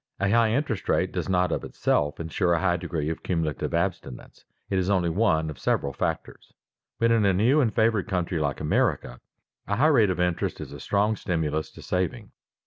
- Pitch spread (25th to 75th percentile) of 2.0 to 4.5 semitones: No, average, 5.1 semitones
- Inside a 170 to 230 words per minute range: Yes, average, 200 wpm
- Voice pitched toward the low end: Yes, very low, 90 Hz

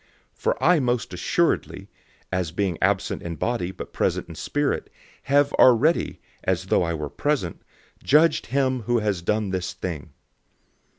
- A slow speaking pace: No, average, 155 wpm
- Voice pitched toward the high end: No, low, 105 Hz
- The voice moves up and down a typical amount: No, wide, 7.1 semitones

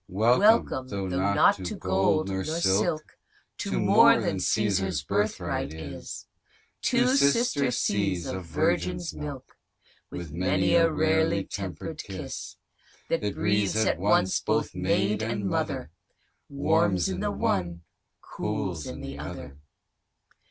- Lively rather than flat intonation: Yes, wide, 5.8 semitones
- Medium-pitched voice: No, low, 100 Hz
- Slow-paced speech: Yes, slow, 120 wpm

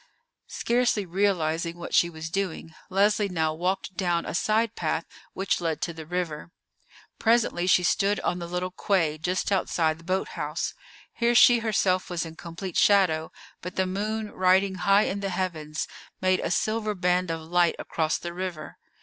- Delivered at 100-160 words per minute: No, average, 170 wpm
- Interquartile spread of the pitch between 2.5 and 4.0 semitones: Yes, average, 3.0 semitones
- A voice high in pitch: No, medium, 180 Hz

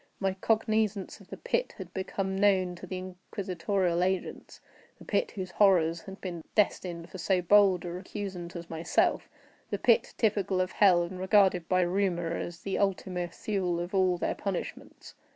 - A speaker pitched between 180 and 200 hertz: Yes, medium, 185 Hz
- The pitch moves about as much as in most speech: No, narrow, 2.0 semitones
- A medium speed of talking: Yes, average, 160 wpm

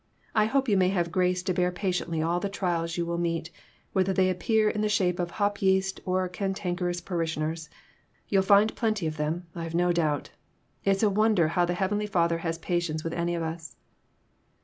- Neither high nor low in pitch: Yes, medium, 180 Hz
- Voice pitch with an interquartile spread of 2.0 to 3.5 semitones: Yes, narrow, 2.5 semitones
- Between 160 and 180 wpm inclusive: No, average, 195 wpm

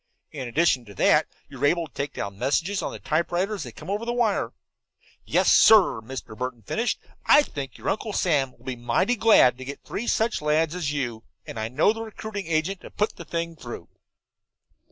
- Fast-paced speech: Yes, fast, 210 wpm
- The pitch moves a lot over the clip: Yes, wide, 7.7 semitones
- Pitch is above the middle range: No, medium, 155 Hz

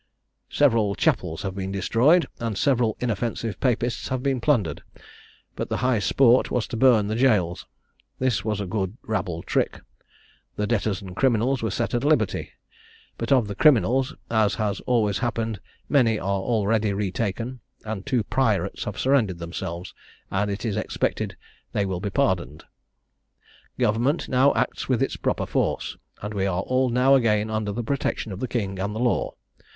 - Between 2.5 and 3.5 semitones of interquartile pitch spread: No, average, 3.9 semitones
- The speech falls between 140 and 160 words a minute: No, average, 170 wpm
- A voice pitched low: Yes, low, 110 Hz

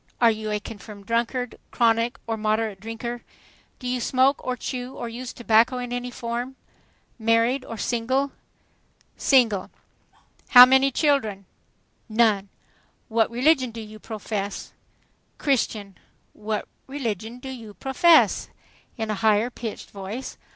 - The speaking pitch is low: No, high, 230 Hz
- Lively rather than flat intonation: No, average, 2.7 semitones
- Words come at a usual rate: No, slow, 130 wpm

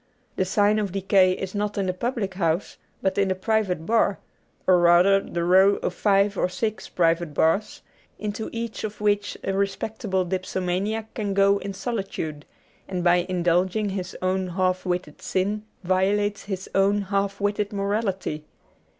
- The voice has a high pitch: Yes, high, 195 Hz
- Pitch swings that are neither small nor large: No, narrow, 2.0 semitones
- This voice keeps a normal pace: Yes, average, 160 wpm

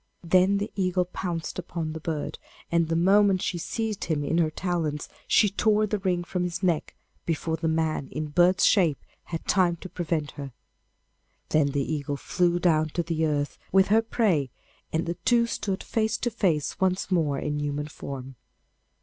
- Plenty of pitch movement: No, average, 3.5 semitones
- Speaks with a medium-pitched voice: Yes, medium, 170 Hz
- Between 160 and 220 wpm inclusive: Yes, average, 180 wpm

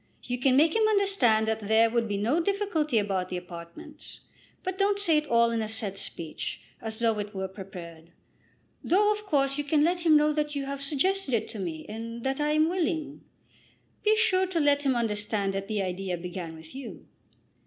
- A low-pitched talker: No, high, 245 Hz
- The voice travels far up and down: Yes, wide, 7.4 semitones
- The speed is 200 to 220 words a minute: Yes, fast, 205 wpm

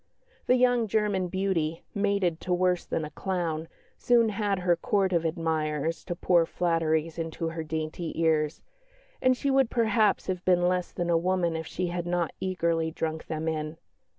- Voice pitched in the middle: Yes, medium, 175 Hz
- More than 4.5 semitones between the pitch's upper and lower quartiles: No, average, 2.8 semitones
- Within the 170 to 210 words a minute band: Yes, average, 175 wpm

